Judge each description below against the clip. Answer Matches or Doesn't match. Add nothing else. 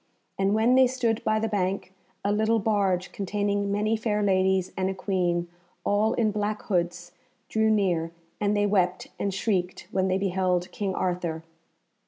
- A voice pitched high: Matches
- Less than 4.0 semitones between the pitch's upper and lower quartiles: Matches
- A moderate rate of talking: Matches